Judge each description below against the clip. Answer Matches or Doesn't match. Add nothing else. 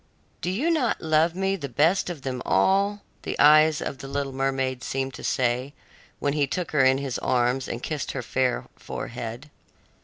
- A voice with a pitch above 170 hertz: Doesn't match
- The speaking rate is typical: Matches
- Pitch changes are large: Doesn't match